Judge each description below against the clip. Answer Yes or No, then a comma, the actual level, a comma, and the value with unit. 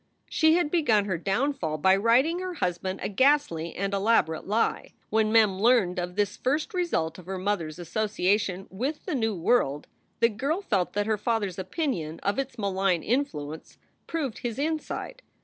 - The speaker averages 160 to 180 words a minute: Yes, average, 175 wpm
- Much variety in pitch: Yes, wide, 6.5 semitones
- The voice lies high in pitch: Yes, high, 210 Hz